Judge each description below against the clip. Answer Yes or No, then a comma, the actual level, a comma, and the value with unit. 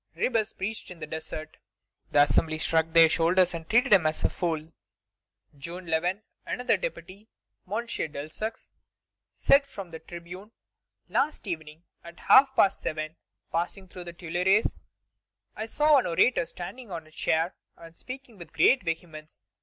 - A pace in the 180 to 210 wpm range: No, average, 150 wpm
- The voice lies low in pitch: No, medium, 175 Hz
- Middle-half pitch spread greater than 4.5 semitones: Yes, average, 5.0 semitones